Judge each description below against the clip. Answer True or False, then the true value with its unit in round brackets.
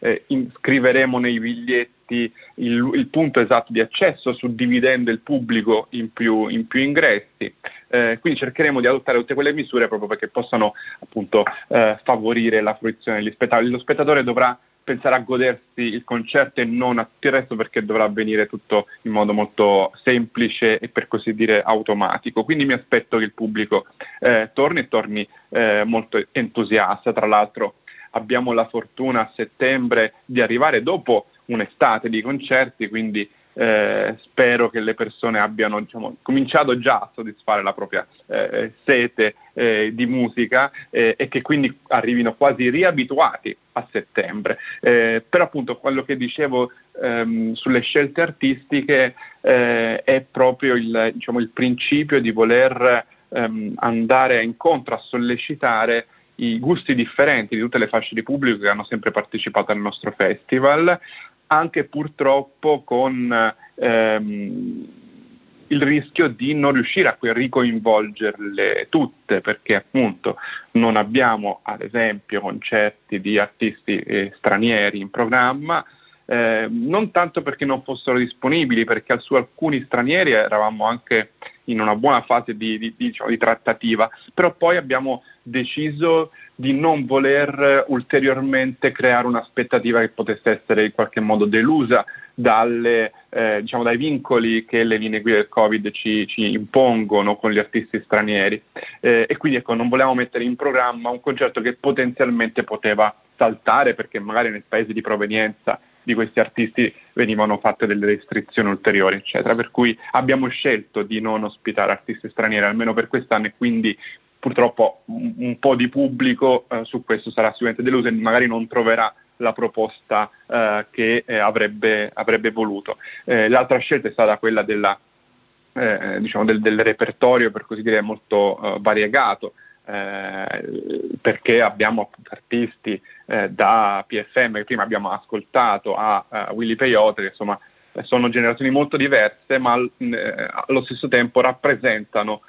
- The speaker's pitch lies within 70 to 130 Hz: True (120 Hz)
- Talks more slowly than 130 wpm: False (150 wpm)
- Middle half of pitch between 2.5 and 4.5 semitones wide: True (3.3 semitones)